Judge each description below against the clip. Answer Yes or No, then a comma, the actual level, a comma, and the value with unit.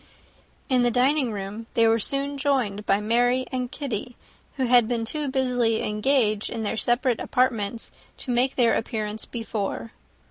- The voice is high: Yes, high, 240 Hz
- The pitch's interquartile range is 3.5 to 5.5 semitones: No, average, 2.7 semitones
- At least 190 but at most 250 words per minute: No, average, 155 wpm